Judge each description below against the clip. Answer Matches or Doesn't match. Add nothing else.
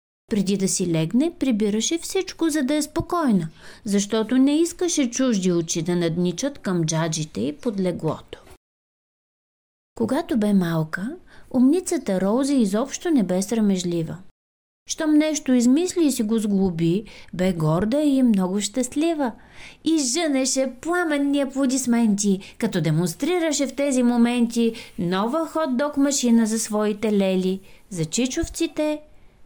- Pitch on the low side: Doesn't match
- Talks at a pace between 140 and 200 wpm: Doesn't match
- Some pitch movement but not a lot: Doesn't match